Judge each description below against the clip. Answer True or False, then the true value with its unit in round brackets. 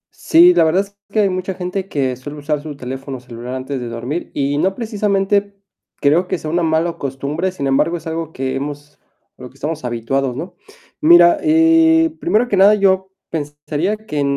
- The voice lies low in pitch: False (160 Hz)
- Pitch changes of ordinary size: False (5.9 semitones)